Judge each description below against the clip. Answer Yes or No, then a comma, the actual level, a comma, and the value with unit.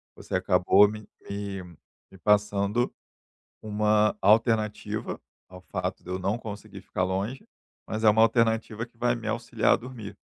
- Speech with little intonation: Yes, narrow, 2.2 semitones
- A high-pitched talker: No, low, 105 Hz